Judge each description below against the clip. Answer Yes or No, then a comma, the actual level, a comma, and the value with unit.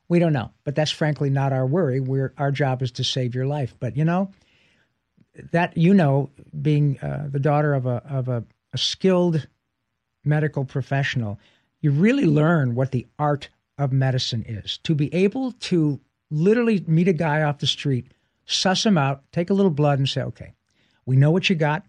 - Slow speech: No, average, 190 wpm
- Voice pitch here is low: No, medium, 145 Hz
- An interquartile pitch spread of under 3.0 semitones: No, average, 4.1 semitones